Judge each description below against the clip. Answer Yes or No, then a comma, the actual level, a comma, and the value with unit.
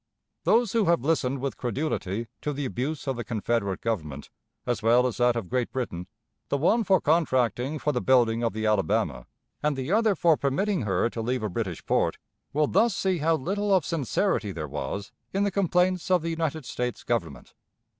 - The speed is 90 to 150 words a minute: No, average, 195 wpm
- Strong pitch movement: Yes, wide, 6.4 semitones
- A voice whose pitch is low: Yes, low, 130 Hz